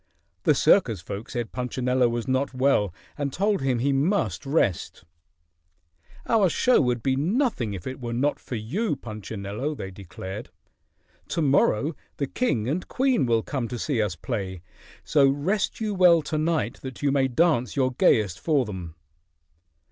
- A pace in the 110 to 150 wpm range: No, average, 165 wpm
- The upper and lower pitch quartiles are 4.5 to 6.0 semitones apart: Yes, wide, 5.5 semitones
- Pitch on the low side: Yes, low, 130 Hz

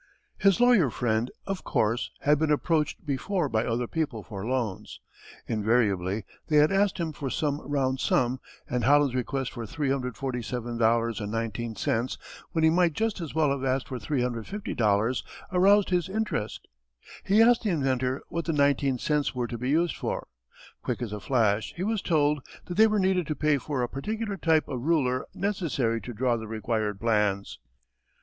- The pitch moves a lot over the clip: Yes, wide, 5.8 semitones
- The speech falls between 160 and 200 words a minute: Yes, average, 170 wpm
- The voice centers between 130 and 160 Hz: Yes, low, 135 Hz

